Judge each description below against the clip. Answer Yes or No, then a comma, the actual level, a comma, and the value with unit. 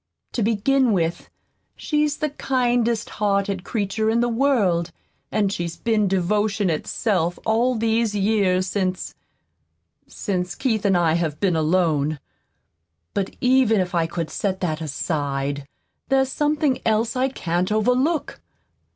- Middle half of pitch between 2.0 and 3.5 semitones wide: No, average, 5.1 semitones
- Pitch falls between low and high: No, high, 205 Hz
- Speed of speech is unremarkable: No, slow, 130 wpm